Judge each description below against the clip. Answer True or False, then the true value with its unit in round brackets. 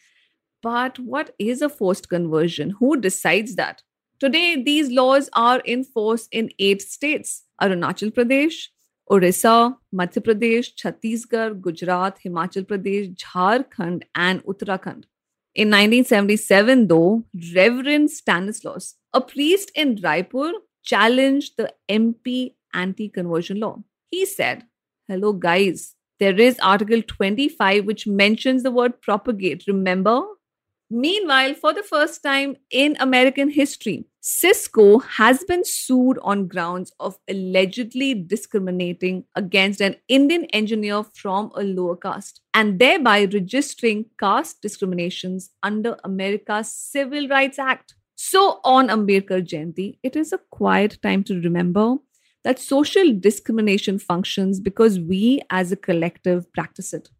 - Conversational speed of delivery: False (120 wpm)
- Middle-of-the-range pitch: False (215 Hz)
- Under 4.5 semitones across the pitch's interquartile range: False (5.4 semitones)